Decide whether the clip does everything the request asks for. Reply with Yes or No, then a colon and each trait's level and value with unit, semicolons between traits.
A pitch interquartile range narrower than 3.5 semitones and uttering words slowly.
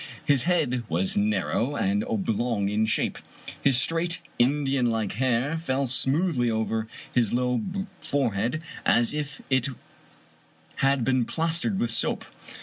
No: average, 4.5 semitones; slow, 130 wpm